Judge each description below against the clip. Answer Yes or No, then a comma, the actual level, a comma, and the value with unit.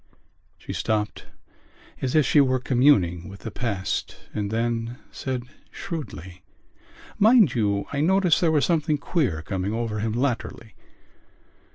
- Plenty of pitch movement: Yes, wide, 6.1 semitones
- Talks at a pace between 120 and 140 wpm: Yes, slow, 135 wpm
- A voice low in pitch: Yes, low, 120 Hz